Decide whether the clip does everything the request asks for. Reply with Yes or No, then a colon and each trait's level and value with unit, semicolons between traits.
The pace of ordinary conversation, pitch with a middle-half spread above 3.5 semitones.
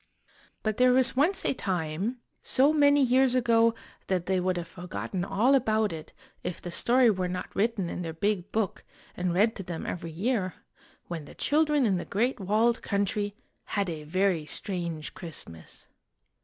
Yes: average, 170 wpm; average, 5.2 semitones